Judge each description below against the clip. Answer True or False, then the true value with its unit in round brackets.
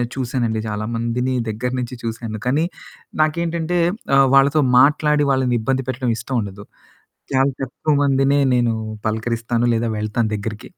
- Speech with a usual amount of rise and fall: True (3.2 semitones)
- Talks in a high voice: False (125 Hz)